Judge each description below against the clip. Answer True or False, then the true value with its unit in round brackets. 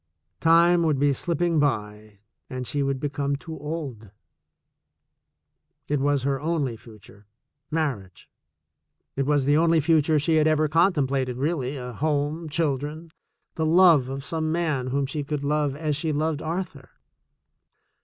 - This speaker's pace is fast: False (155 wpm)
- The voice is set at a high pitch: False (145 Hz)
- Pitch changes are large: False (2.8 semitones)